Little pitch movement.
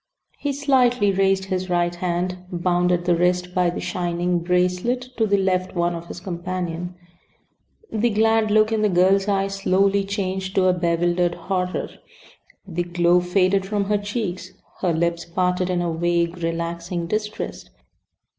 Yes: narrow, 2.2 semitones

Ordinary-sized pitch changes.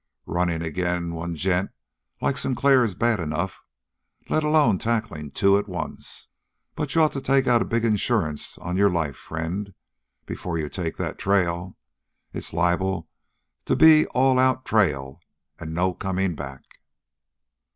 No: wide, 5.7 semitones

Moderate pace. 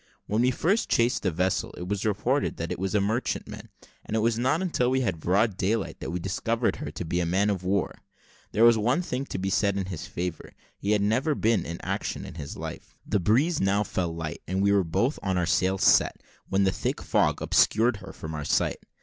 No: fast, 235 wpm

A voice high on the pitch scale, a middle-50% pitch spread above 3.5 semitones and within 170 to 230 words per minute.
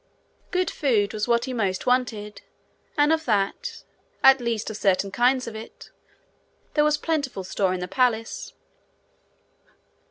No: high, 235 Hz; average, 4.6 semitones; average, 140 wpm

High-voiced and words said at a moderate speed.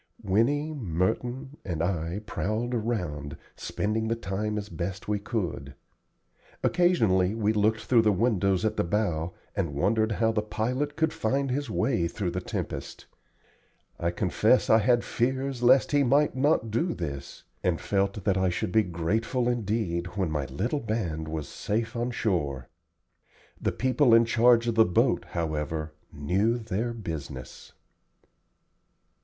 No: low, 105 Hz; average, 150 wpm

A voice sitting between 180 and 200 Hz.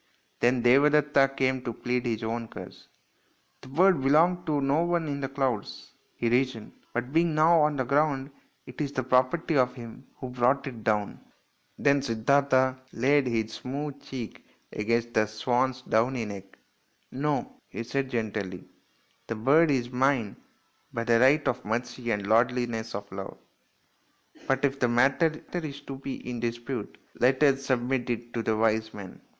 No: low, 130 Hz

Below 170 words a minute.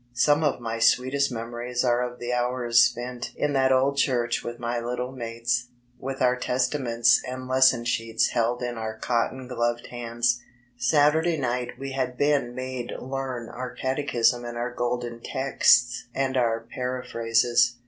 Yes: average, 160 wpm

